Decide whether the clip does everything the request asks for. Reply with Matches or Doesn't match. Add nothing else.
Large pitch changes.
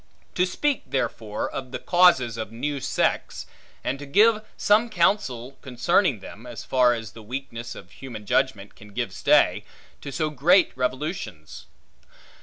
Matches